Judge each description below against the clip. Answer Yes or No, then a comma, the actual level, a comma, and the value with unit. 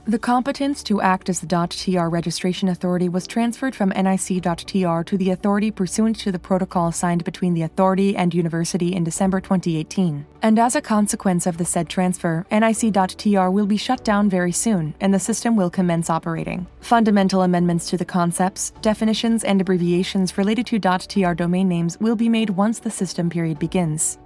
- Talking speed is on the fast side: No, average, 175 wpm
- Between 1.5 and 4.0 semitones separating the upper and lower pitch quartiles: Yes, average, 3.1 semitones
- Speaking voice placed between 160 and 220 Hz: Yes, medium, 185 Hz